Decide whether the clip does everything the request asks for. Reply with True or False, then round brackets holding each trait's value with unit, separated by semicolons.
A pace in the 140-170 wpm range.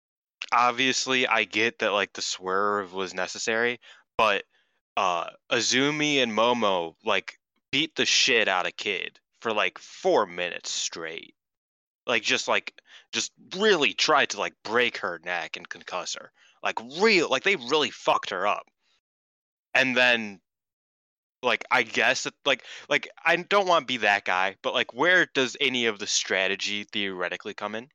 True (160 wpm)